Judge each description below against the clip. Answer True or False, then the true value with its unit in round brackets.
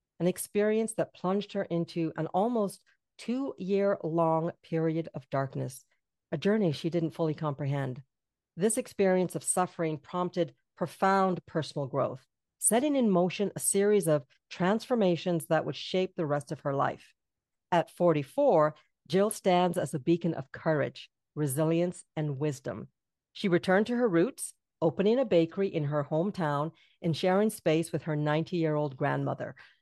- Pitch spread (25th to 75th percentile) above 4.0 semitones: False (3.6 semitones)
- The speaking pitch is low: False (170 Hz)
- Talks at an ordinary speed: True (150 wpm)